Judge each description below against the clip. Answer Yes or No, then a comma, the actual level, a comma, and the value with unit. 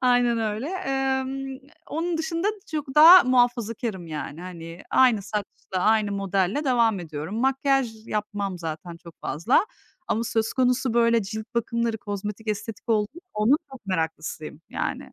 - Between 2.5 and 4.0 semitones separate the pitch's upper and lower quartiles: No, average, 4.8 semitones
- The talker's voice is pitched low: No, high, 225 Hz